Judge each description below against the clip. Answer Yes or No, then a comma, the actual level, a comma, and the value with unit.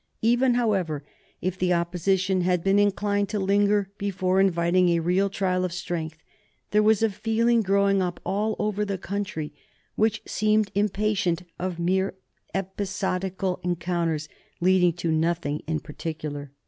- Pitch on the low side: No, high, 190 Hz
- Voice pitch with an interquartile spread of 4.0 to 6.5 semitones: No, average, 2.8 semitones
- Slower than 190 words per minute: Yes, average, 140 wpm